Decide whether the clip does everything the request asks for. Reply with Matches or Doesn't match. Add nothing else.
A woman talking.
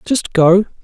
Doesn't match